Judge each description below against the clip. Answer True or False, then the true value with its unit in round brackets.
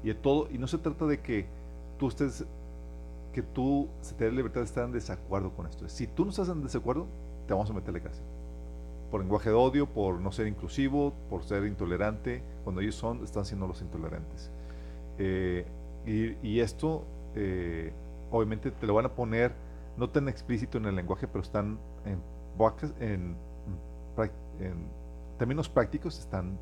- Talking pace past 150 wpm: True (170 wpm)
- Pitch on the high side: False (95 Hz)